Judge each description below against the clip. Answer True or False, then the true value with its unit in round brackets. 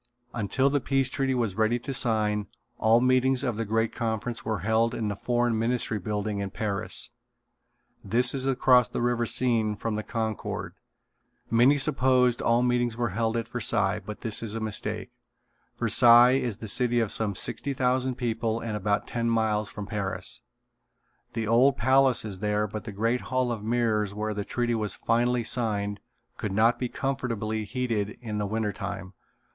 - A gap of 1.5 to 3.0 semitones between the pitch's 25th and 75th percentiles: True (2.5 semitones)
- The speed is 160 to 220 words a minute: True (175 wpm)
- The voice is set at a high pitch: False (115 Hz)